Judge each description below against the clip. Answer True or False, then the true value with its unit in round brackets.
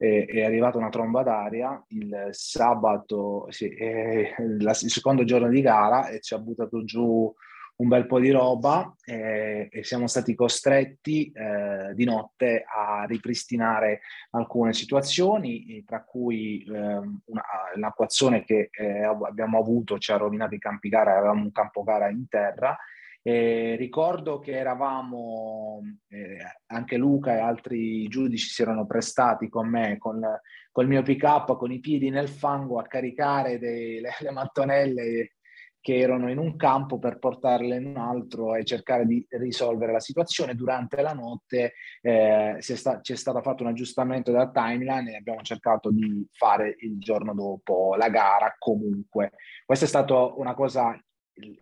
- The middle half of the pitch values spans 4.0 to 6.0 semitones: False (2.9 semitones)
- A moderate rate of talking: True (155 wpm)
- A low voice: True (120 Hz)